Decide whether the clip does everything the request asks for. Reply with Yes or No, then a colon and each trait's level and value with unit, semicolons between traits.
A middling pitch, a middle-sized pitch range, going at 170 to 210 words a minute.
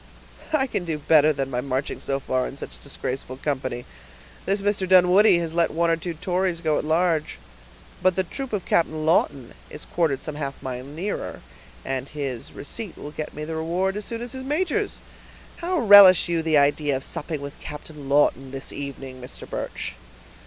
Yes: medium, 155 Hz; average, 4.9 semitones; average, 190 wpm